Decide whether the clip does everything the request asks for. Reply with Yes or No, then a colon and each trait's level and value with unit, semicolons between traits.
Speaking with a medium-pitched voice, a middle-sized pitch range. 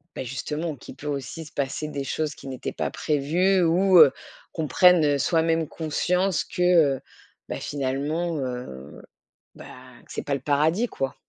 Yes: medium, 150 Hz; average, 3.6 semitones